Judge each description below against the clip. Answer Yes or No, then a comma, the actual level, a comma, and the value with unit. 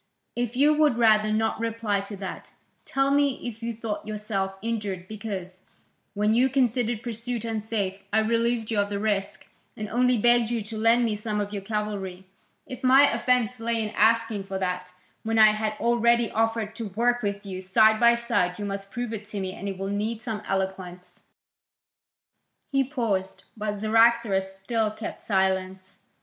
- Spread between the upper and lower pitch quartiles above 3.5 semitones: No, average, 2.8 semitones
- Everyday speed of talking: Yes, average, 175 wpm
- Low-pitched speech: No, high, 215 Hz